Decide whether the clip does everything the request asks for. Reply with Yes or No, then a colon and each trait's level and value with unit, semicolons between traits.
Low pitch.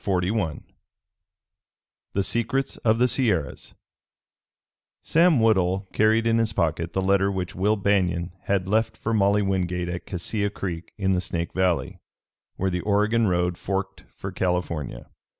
Yes: very low, 95 Hz